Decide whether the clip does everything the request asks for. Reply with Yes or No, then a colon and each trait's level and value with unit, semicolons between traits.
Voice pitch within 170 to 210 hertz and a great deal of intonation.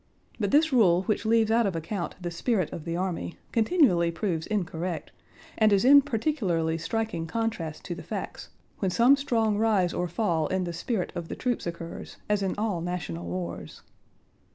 No: high, 190 Hz; average, 5.0 semitones